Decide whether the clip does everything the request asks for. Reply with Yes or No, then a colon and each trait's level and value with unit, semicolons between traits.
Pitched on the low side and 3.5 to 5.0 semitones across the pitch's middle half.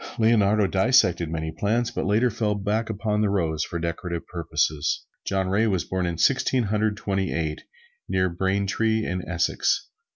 Yes: very low, 95 Hz; average, 3.9 semitones